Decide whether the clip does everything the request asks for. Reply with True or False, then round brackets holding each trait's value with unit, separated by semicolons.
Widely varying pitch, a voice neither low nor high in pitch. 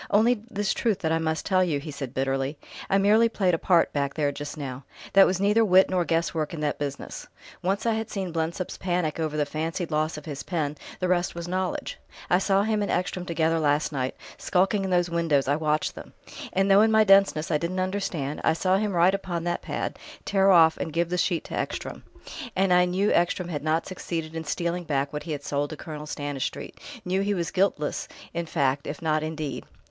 False (3.8 semitones; 170 Hz)